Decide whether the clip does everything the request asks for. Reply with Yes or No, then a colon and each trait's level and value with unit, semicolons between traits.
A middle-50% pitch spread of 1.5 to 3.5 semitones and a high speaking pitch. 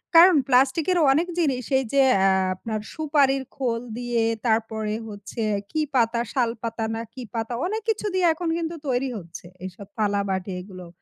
No: average, 5.1 semitones; high, 240 Hz